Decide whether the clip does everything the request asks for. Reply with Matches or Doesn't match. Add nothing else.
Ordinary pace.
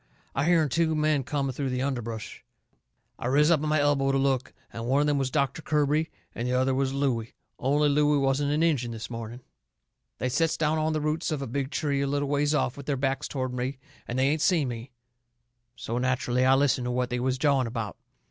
Doesn't match